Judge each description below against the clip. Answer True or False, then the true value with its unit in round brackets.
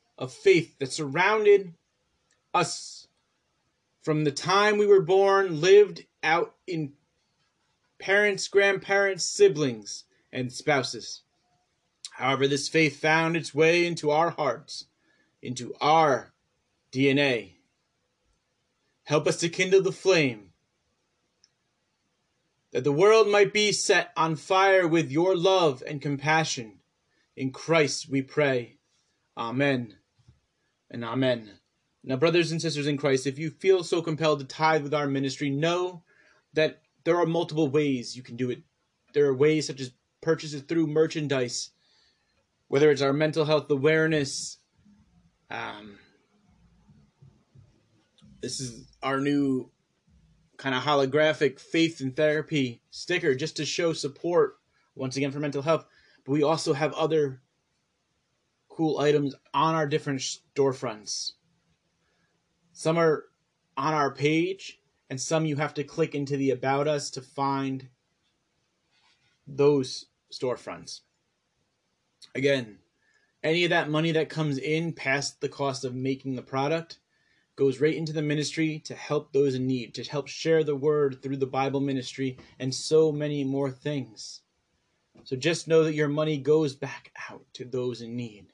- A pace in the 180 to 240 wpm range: False (135 wpm)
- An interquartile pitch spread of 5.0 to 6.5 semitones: False (3.3 semitones)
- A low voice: False (150 Hz)